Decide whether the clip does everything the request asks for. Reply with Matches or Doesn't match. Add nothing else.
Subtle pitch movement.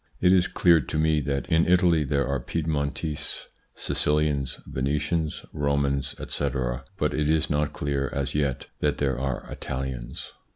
Matches